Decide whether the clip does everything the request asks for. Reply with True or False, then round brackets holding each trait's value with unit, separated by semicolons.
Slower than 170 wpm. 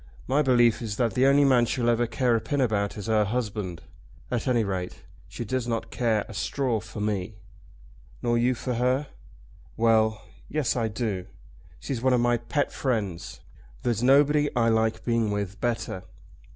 False (175 wpm)